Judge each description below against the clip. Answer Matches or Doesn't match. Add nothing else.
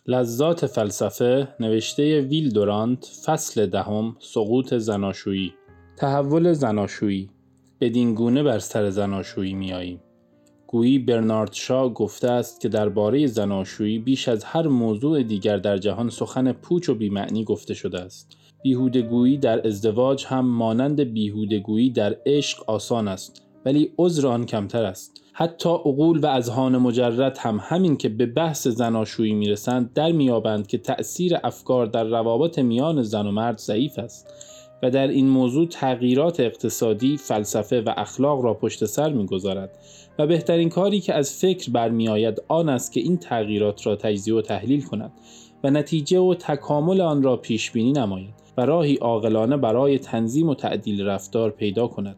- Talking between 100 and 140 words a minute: Doesn't match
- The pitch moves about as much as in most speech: Matches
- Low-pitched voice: Matches